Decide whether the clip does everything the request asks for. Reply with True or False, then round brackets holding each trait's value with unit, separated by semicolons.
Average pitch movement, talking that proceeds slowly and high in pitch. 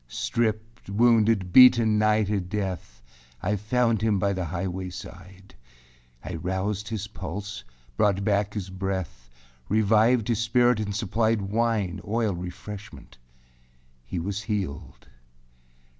False (3.1 semitones; 120 wpm; 100 Hz)